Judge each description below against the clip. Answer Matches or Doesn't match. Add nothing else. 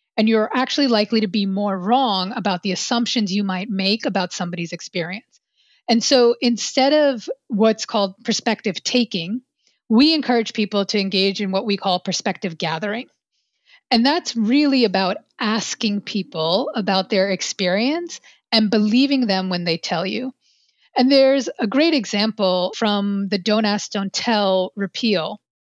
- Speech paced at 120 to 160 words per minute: Matches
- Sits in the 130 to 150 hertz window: Doesn't match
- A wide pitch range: Doesn't match